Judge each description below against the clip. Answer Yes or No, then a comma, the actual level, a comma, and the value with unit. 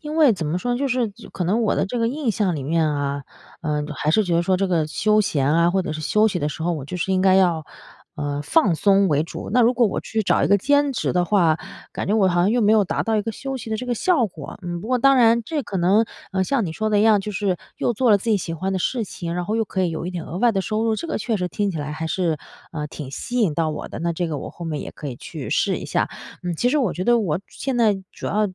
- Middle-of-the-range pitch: No, high, 195 Hz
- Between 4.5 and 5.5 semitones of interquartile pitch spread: Yes, average, 5.2 semitones